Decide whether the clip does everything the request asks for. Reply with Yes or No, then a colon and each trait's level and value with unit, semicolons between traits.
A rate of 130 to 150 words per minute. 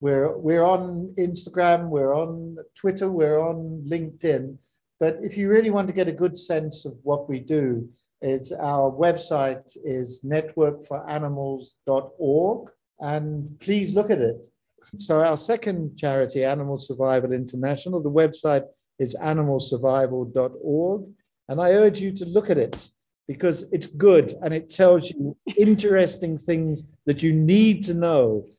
Yes: average, 140 wpm